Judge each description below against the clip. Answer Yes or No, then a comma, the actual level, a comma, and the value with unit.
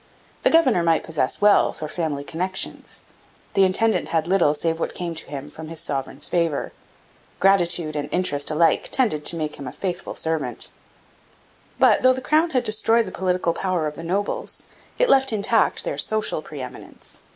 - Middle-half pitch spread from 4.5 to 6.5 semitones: Yes, average, 5.0 semitones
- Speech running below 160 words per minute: No, average, 175 wpm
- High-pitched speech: No, medium, 170 Hz